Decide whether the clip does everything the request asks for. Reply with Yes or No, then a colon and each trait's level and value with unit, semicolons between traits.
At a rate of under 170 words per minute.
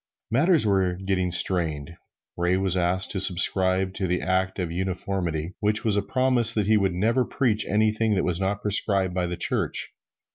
No: average, 180 wpm